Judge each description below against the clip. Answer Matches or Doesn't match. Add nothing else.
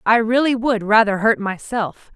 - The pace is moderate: Matches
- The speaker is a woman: Matches